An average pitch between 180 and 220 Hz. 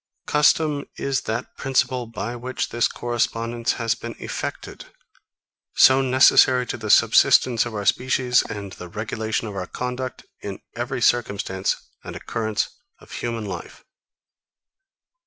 No: low, 120 Hz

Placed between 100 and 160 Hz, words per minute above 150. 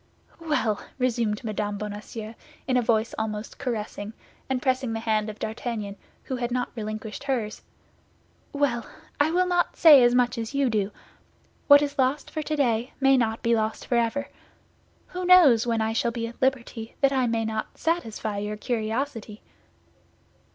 No: high, 235 Hz; average, 160 wpm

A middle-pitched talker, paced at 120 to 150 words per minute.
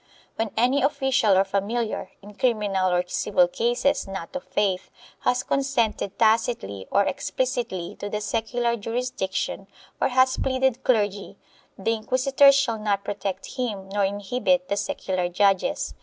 No: high, 215 Hz; average, 140 wpm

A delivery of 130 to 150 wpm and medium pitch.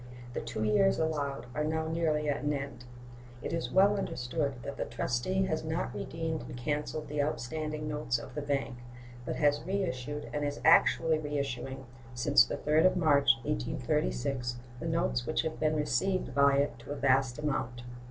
No: average, 175 wpm; medium, 145 Hz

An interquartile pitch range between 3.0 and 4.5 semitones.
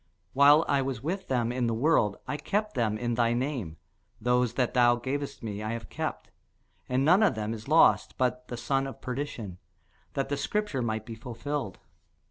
Yes: average, 3.4 semitones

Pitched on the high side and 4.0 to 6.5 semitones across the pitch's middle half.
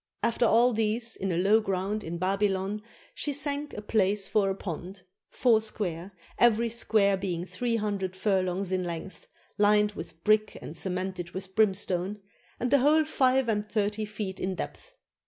No: high, 205 Hz; average, 2.9 semitones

